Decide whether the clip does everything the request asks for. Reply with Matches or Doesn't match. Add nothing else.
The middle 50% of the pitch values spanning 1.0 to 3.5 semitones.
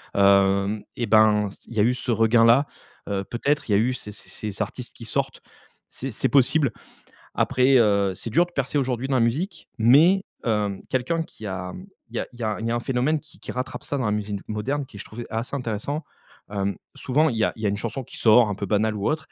Doesn't match